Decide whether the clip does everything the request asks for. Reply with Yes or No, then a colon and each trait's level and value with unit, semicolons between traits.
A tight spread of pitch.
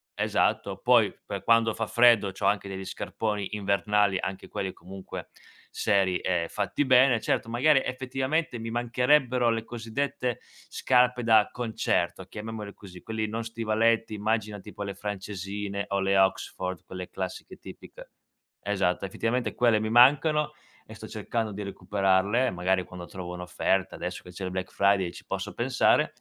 No: average, 3.5 semitones